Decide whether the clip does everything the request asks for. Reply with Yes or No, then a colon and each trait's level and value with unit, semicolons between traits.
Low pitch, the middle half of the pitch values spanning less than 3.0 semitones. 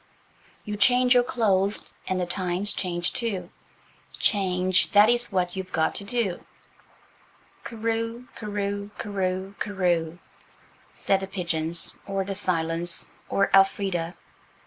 No: high, 195 Hz; narrow, 2.5 semitones